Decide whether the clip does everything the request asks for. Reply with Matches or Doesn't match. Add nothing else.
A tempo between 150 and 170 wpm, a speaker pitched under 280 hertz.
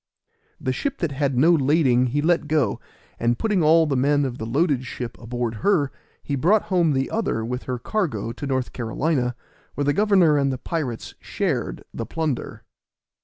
Doesn't match